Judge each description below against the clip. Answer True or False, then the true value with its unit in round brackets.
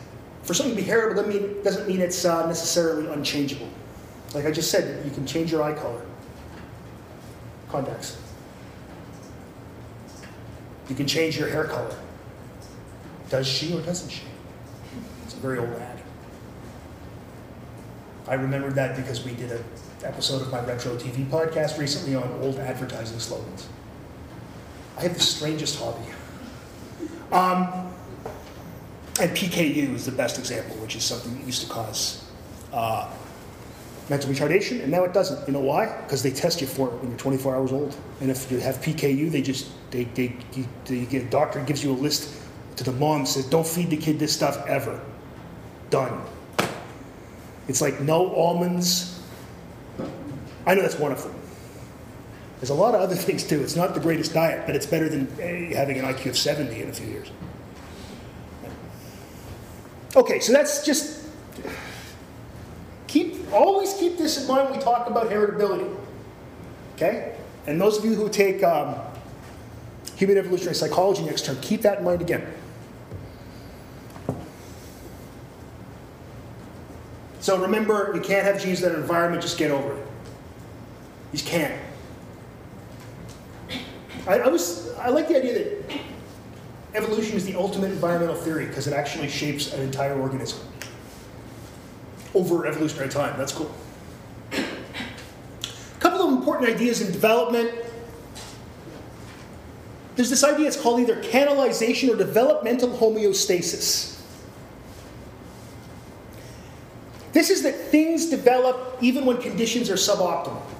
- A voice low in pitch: False (155 Hz)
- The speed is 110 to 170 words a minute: True (145 wpm)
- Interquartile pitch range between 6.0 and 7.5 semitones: True (7.0 semitones)